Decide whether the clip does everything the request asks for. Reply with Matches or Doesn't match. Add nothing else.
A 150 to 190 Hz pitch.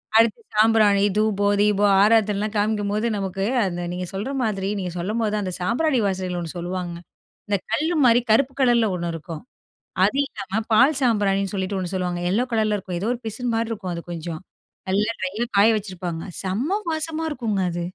Doesn't match